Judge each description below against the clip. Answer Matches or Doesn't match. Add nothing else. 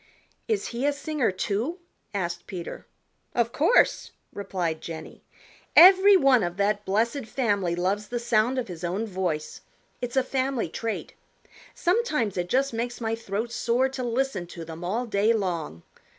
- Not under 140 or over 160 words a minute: Matches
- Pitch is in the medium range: Doesn't match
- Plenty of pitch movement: Matches